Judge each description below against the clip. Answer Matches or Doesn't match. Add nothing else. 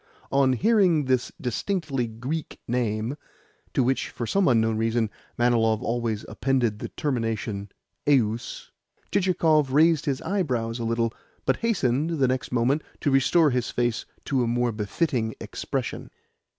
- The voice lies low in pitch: Matches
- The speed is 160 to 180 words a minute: Doesn't match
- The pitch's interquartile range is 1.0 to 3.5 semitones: Doesn't match